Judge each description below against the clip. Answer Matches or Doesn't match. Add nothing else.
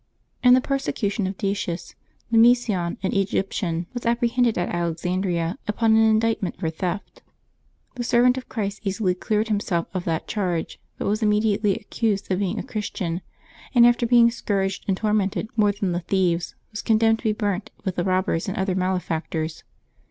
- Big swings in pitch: Doesn't match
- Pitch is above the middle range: Matches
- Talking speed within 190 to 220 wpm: Doesn't match